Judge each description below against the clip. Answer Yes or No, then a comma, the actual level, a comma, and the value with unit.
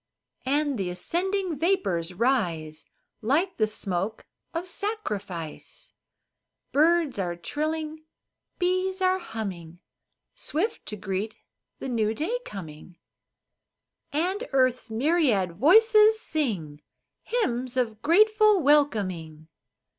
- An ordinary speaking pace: No, slow, 95 wpm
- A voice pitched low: No, very high, 265 Hz